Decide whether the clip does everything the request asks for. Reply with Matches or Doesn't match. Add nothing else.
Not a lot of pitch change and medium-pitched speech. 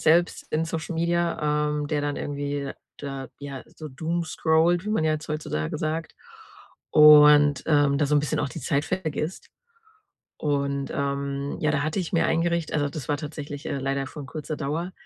Matches